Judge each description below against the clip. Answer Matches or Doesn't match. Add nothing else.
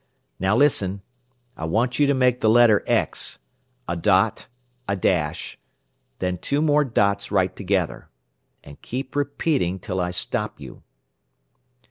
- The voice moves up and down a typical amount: Doesn't match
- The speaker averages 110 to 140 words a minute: Matches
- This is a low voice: Matches